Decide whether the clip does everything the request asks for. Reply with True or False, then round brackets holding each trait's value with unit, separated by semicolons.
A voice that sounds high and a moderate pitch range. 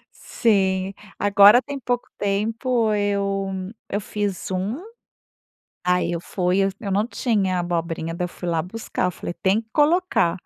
True (200 Hz; 3.6 semitones)